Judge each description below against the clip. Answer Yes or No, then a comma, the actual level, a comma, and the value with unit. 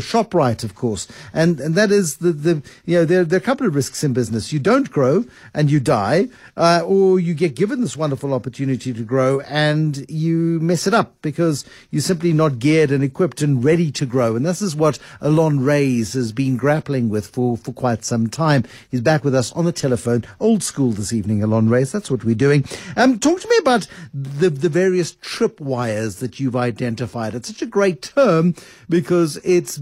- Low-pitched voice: No, medium, 150 Hz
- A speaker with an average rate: No, fast, 210 wpm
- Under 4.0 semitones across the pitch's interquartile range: No, wide, 5.6 semitones